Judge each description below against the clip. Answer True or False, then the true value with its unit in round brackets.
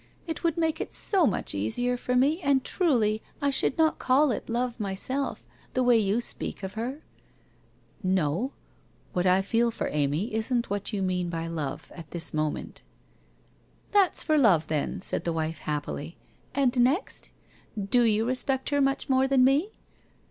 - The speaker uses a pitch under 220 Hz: False (235 Hz)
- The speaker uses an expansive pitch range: True (6.7 semitones)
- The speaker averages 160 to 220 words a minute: True (180 wpm)